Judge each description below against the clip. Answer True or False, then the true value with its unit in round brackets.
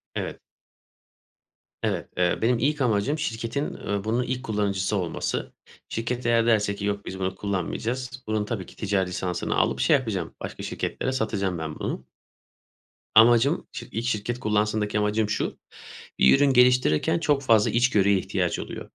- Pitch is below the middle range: True (110 Hz)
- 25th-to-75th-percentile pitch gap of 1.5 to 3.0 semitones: False (3.6 semitones)